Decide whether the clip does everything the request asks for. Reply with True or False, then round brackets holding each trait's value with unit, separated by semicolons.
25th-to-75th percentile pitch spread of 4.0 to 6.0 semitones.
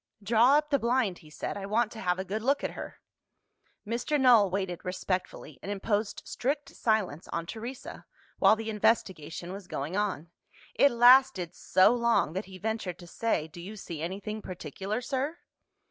True (4.5 semitones)